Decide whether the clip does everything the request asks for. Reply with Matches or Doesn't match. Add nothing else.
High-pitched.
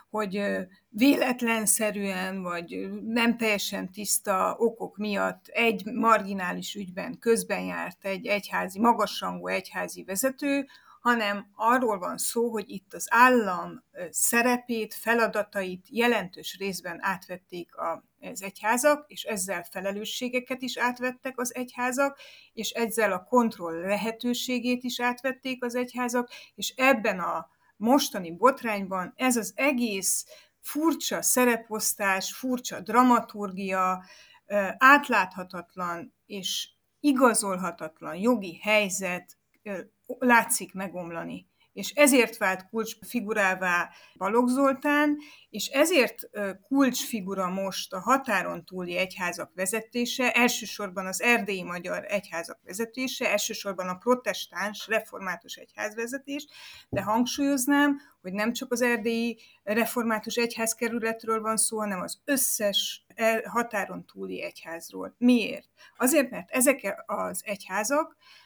Matches